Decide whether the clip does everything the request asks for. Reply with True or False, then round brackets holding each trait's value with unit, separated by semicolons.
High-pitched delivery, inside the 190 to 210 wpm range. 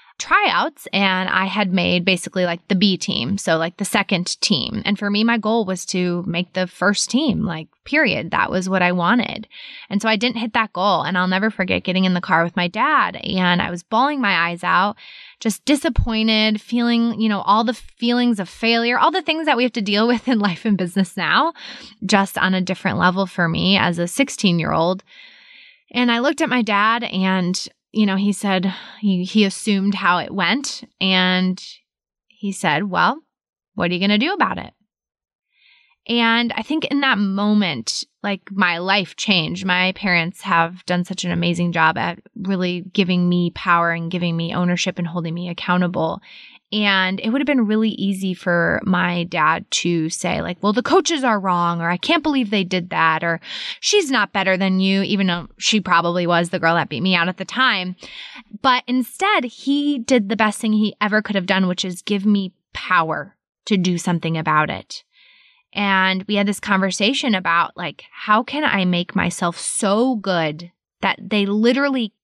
True (195 Hz; 200 wpm)